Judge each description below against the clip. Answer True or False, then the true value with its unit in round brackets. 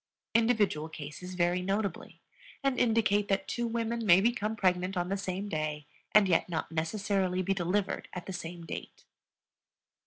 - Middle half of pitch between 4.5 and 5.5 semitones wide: False (3.3 semitones)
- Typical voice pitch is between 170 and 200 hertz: True (190 Hz)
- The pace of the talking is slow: False (155 wpm)